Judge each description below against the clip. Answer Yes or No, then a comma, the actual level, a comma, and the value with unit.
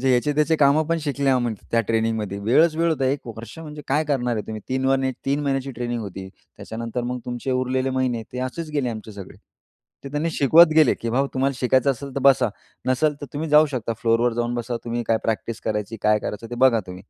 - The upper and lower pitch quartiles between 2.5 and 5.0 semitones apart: Yes, average, 3.4 semitones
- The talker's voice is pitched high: No, low, 130 Hz